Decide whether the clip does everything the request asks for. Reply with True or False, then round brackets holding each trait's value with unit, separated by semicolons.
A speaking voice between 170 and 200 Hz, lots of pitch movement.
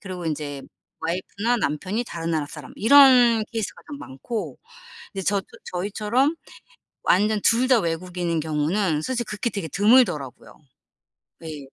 True (190 Hz; 6.0 semitones)